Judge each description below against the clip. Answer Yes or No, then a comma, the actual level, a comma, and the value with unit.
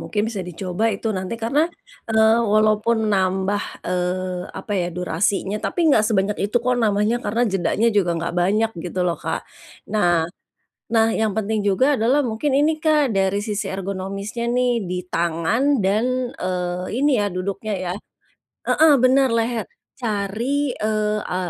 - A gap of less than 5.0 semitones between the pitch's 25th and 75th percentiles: Yes, average, 3.2 semitones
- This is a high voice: Yes, high, 205 Hz